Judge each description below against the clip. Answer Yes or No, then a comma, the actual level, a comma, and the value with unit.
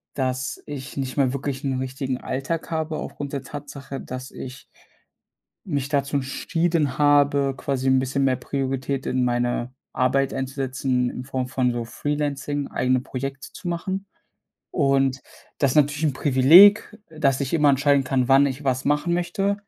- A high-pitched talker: No, low, 135 Hz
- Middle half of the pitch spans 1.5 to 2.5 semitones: Yes, narrow, 2.0 semitones